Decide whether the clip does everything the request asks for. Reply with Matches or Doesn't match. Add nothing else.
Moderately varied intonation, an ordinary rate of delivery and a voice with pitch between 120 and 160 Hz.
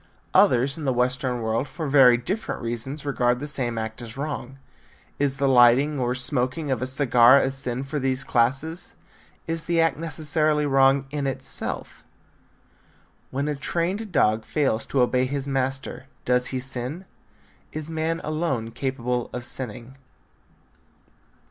Matches